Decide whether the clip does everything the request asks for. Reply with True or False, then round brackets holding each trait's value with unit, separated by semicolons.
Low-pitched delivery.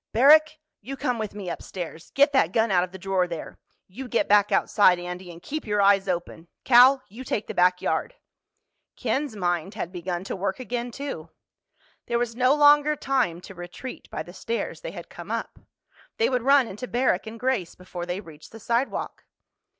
False (215 Hz)